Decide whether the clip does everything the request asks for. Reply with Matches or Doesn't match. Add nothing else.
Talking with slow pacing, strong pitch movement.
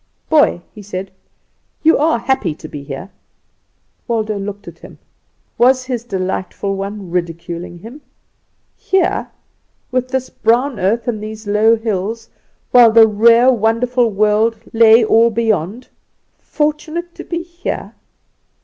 Doesn't match